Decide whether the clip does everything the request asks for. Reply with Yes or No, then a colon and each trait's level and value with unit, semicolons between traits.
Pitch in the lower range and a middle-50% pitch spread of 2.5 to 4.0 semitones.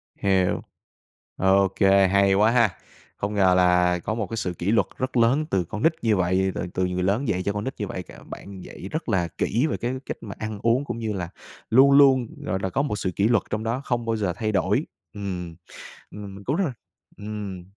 Yes: low, 100 Hz; average, 3.6 semitones